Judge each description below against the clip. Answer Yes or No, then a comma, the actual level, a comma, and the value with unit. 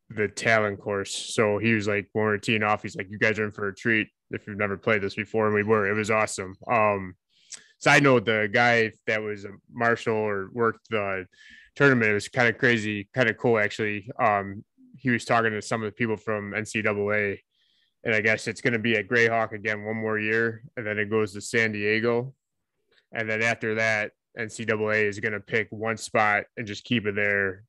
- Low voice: Yes, low, 110 Hz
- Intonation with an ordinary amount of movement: No, narrow, 1.8 semitones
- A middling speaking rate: No, fast, 215 wpm